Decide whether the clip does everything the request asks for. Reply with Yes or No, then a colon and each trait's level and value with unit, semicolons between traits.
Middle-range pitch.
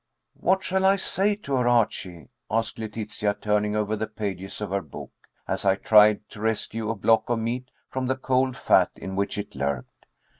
No: low, 110 Hz